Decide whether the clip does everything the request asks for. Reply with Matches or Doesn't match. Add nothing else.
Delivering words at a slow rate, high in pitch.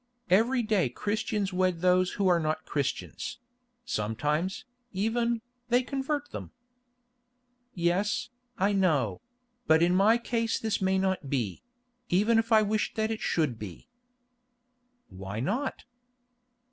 Matches